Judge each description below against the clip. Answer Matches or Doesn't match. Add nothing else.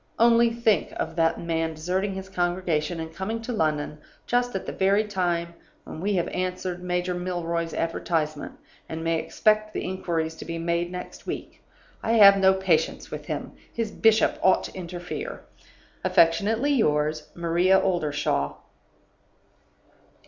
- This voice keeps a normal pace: Matches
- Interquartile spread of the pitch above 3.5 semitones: Doesn't match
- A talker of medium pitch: Matches